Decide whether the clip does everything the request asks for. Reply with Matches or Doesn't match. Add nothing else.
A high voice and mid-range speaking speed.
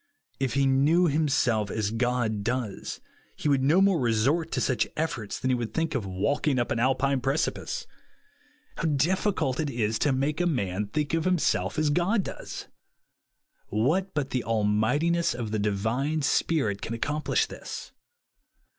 Doesn't match